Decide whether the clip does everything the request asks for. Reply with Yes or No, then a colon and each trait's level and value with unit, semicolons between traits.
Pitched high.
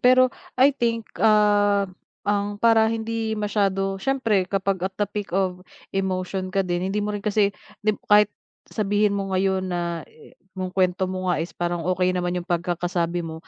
Yes: high, 195 Hz